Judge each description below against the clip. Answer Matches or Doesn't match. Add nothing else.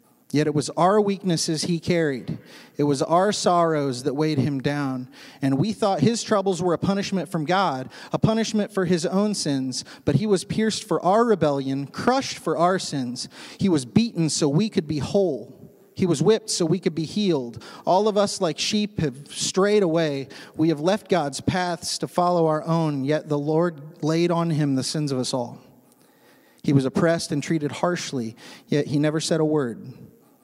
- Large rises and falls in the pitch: Doesn't match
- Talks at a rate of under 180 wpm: Doesn't match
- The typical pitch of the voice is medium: Matches